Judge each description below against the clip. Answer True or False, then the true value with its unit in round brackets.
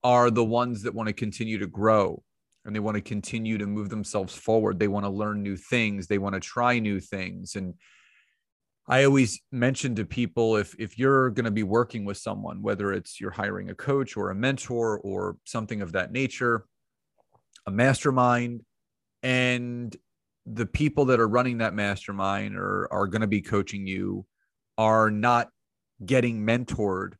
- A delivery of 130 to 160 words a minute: False (175 wpm)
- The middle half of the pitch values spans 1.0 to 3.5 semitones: True (3.1 semitones)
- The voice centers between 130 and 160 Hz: False (110 Hz)